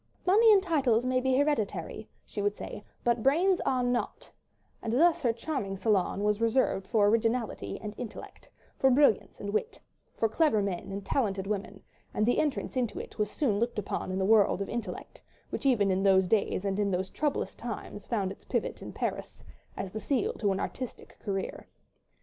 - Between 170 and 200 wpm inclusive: Yes, average, 185 wpm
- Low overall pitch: No, high, 220 Hz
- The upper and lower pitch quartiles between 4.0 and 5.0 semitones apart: Yes, average, 4.4 semitones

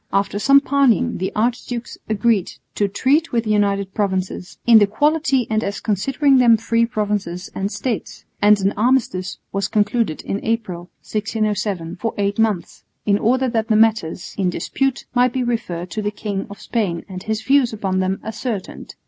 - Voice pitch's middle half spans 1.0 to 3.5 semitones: Yes, average, 3.2 semitones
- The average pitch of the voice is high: Yes, high, 215 Hz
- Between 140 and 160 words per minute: No, average, 175 wpm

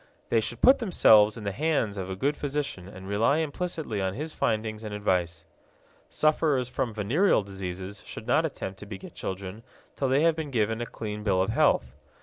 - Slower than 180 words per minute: No, average, 190 wpm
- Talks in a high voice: No, low, 110 Hz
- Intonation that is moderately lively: No, wide, 6.7 semitones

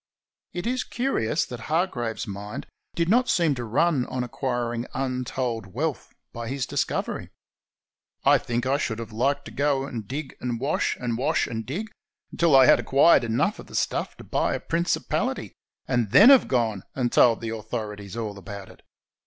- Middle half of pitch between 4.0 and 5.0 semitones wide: Yes, average, 4.3 semitones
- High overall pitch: No, low, 125 Hz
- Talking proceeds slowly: No, average, 175 wpm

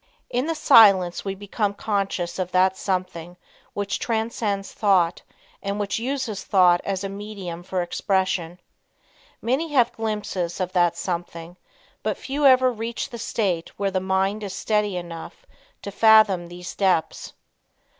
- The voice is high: Yes, high, 195 Hz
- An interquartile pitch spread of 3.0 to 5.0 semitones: Yes, average, 3.3 semitones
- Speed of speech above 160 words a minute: No, average, 145 wpm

